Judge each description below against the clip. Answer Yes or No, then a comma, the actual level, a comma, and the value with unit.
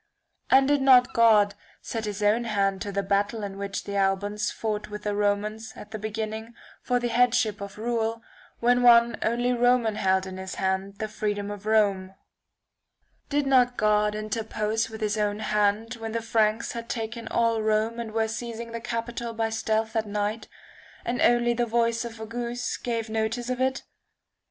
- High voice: Yes, high, 220 Hz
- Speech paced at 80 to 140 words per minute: No, average, 185 wpm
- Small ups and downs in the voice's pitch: Yes, narrow, 2.1 semitones